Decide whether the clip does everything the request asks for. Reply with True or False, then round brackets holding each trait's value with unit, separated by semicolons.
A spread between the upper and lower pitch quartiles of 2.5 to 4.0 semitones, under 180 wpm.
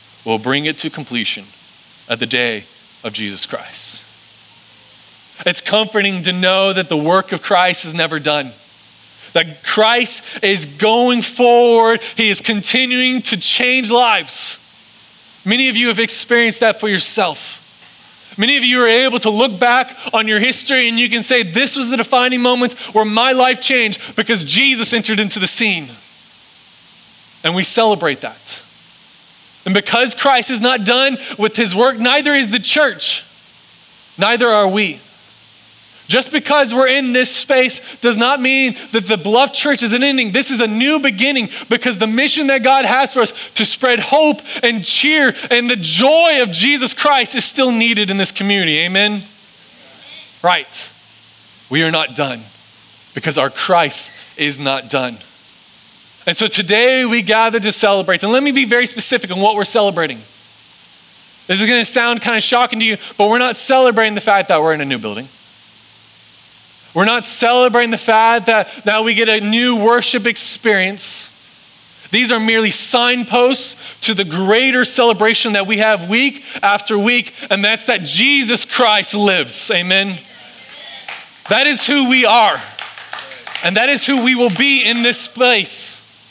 False (4.4 semitones; 165 wpm)